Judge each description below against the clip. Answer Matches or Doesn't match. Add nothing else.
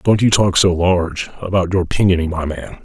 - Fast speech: Matches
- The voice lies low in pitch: Matches